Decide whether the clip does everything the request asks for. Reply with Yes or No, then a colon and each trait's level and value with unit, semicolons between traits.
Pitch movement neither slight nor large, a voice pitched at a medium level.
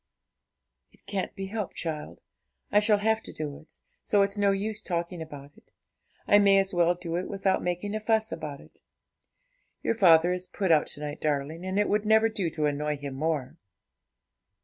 Yes: average, 4.7 semitones; medium, 180 Hz